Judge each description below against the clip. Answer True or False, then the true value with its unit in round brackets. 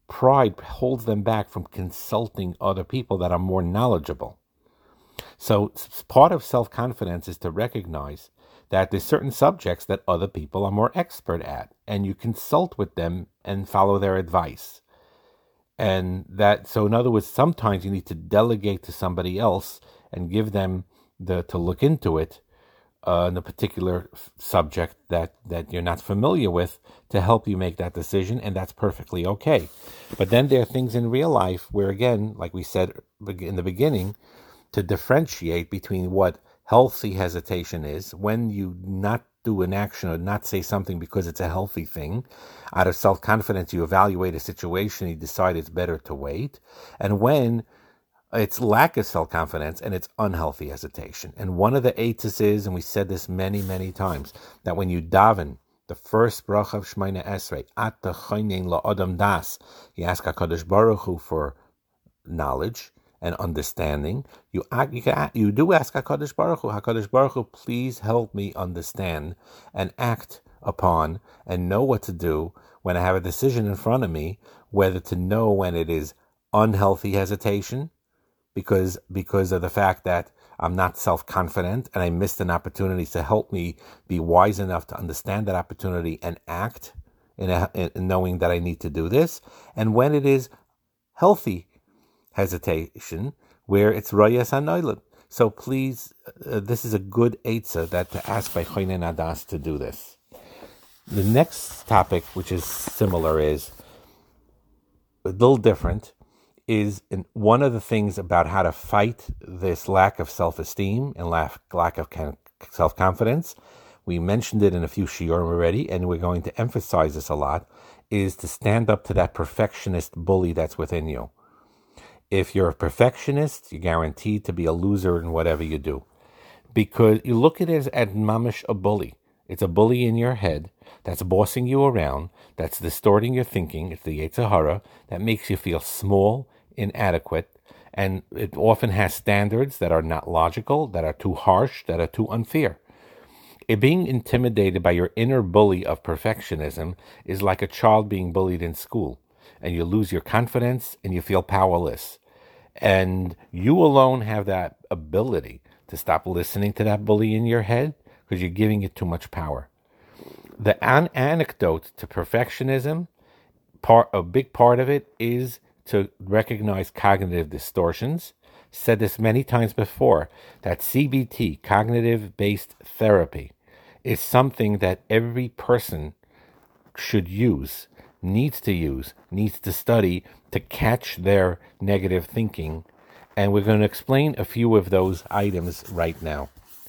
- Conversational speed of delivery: True (165 wpm)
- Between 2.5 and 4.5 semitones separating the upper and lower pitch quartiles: True (4.1 semitones)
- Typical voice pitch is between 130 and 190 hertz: False (100 Hz)